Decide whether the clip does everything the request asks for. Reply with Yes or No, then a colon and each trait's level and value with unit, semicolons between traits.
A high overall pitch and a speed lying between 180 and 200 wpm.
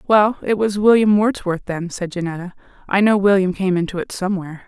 Yes: high, 195 Hz; average, 190 wpm